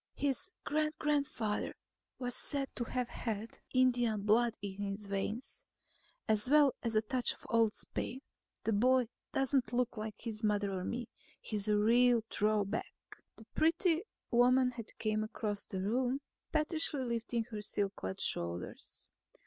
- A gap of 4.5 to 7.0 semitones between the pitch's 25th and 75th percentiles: No, average, 3.4 semitones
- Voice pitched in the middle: No, high, 230 Hz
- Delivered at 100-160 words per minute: Yes, average, 150 wpm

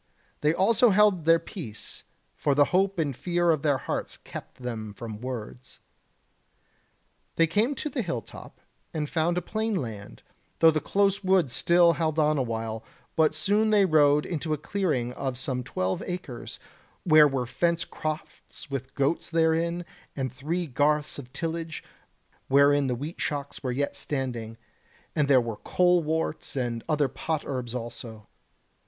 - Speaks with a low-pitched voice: No, medium, 150 Hz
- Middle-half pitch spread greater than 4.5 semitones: Yes, average, 5.1 semitones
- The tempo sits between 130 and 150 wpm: No, average, 160 wpm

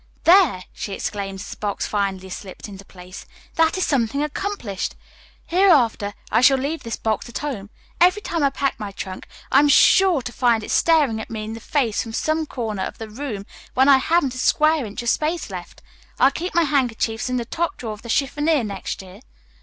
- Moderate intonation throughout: No, wide, 6.1 semitones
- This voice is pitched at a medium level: No, very high, 250 Hz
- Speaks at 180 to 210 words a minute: Yes, fast, 205 wpm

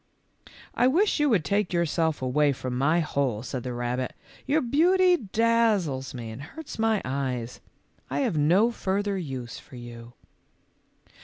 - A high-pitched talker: No, medium, 160 Hz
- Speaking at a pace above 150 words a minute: Yes, average, 165 wpm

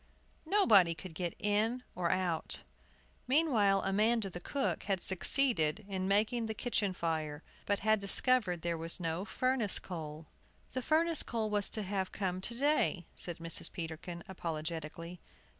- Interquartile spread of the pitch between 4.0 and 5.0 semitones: Yes, average, 4.6 semitones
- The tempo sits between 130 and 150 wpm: Yes, average, 145 wpm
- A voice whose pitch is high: Yes, high, 195 Hz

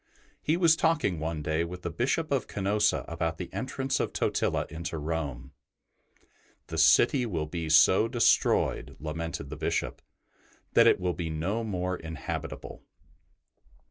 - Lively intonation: Yes, wide, 5.9 semitones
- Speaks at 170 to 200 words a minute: No, average, 145 wpm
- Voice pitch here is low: Yes, very low, 85 Hz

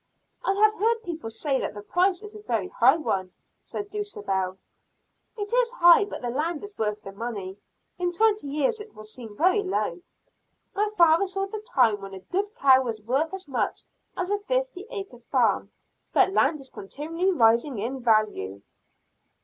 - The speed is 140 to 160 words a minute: No, average, 175 wpm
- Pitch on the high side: Yes, very high, 305 Hz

